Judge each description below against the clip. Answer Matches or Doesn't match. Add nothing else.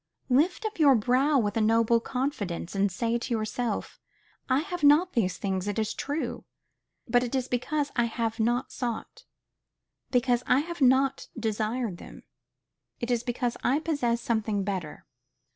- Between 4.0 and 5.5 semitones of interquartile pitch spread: Doesn't match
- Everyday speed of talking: Matches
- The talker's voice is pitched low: Doesn't match